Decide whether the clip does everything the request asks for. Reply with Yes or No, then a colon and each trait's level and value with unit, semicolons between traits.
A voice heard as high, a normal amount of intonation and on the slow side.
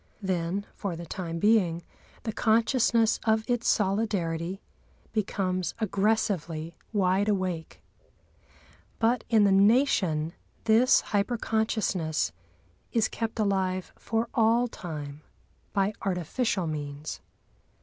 Yes: high, 200 Hz; average, 4.5 semitones; slow, 100 wpm